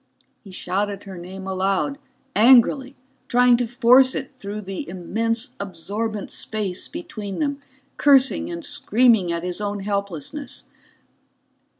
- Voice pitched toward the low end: No, high, 210 Hz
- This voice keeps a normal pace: No, slow, 125 wpm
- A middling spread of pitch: Yes, average, 4.6 semitones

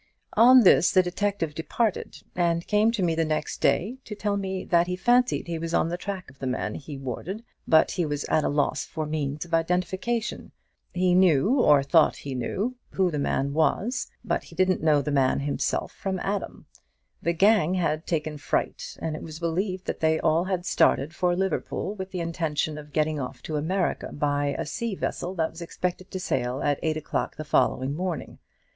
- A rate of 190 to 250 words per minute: Yes, average, 200 wpm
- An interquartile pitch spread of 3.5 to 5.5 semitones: Yes, average, 3.9 semitones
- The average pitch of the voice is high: No, medium, 170 Hz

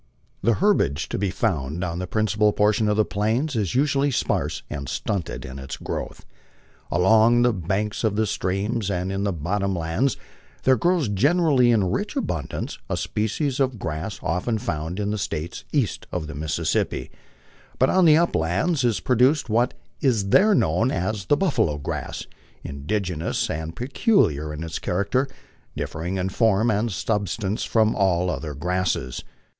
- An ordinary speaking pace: Yes, average, 160 wpm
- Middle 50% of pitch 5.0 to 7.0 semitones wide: Yes, wide, 5.4 semitones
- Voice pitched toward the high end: No, low, 105 Hz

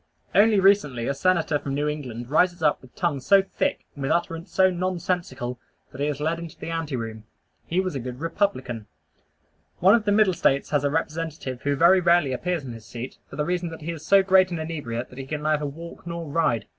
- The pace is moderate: No, fast, 220 wpm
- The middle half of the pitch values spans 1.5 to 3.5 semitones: No, average, 4.7 semitones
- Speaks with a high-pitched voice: No, medium, 160 Hz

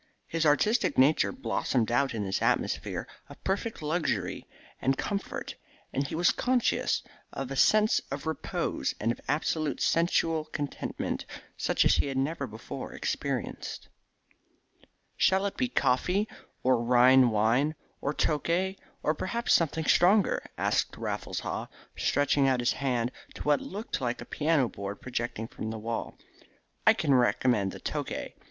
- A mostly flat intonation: No, average, 5.2 semitones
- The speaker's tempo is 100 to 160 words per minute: Yes, average, 145 wpm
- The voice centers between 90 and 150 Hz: Yes, medium, 140 Hz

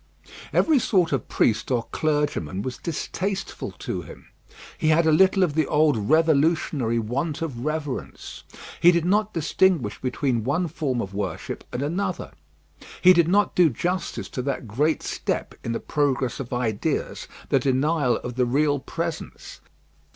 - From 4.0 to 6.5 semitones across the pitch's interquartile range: Yes, average, 5.1 semitones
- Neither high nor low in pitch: Yes, medium, 150 Hz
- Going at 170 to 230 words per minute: No, average, 155 wpm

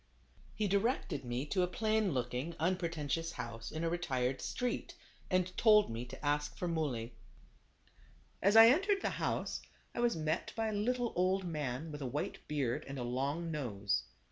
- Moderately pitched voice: Yes, medium, 160 Hz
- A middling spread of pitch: No, wide, 7.0 semitones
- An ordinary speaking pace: Yes, average, 170 wpm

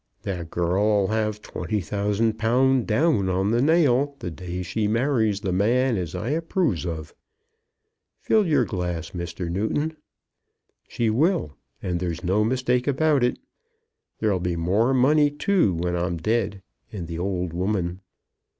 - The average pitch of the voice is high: No, low, 105 Hz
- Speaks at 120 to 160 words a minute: Yes, average, 150 wpm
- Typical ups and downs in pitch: No, wide, 6.1 semitones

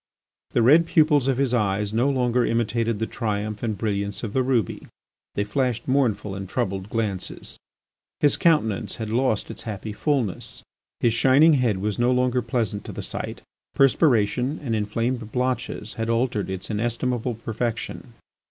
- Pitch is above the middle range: No, low, 115 Hz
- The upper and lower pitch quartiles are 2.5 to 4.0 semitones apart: Yes, average, 3.2 semitones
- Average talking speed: Yes, average, 155 wpm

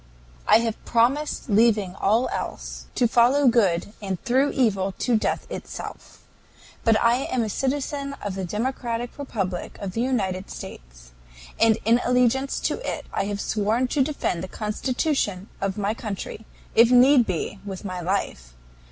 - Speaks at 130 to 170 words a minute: Yes, average, 155 wpm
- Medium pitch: No, high, 225 Hz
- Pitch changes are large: No, average, 4.3 semitones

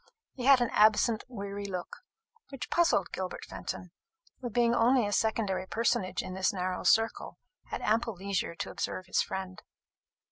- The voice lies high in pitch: Yes, high, 205 Hz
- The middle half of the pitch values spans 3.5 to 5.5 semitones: Yes, average, 3.9 semitones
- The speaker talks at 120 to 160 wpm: Yes, average, 155 wpm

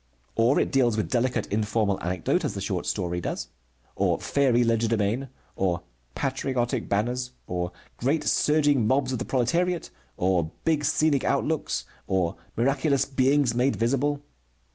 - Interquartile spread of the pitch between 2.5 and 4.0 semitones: No, average, 4.5 semitones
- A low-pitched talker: Yes, low, 125 Hz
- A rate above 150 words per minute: No, average, 140 wpm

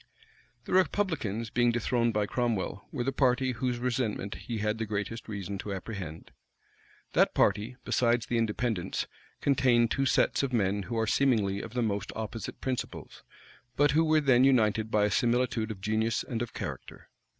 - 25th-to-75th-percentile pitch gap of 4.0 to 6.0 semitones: No, average, 3.0 semitones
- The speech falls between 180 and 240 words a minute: No, average, 170 wpm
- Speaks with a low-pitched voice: Yes, low, 115 Hz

